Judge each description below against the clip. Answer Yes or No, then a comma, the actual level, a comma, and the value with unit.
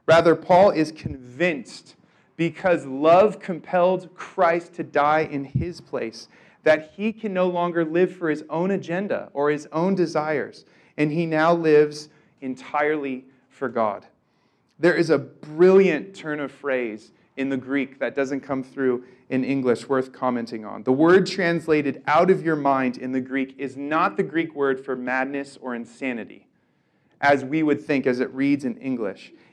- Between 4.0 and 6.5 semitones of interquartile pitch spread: Yes, average, 4.4 semitones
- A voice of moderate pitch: Yes, medium, 150 Hz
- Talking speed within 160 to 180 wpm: Yes, average, 165 wpm